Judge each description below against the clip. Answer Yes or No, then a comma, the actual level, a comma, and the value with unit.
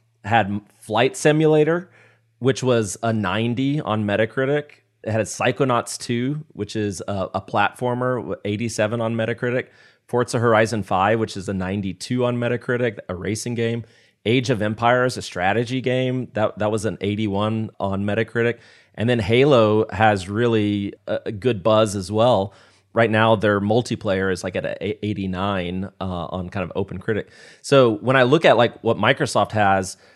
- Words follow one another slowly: No, average, 165 wpm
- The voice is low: Yes, low, 110 Hz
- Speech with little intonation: No, average, 3.3 semitones